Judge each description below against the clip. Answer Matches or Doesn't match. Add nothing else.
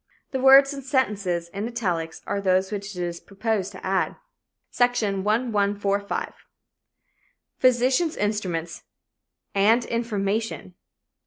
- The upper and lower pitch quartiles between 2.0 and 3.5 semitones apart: Doesn't match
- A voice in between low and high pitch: Doesn't match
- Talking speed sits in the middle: Doesn't match